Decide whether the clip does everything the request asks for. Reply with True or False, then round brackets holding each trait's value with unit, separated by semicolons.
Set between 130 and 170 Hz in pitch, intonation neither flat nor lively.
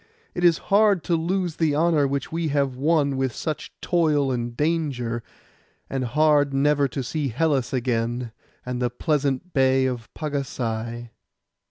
True (140 Hz; 3.9 semitones)